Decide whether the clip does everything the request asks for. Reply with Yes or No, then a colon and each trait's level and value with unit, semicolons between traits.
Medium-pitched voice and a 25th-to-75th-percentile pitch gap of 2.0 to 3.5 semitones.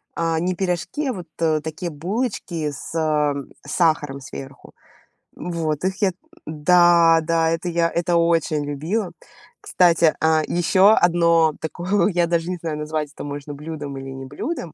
Yes: medium, 165 Hz; narrow, 2.4 semitones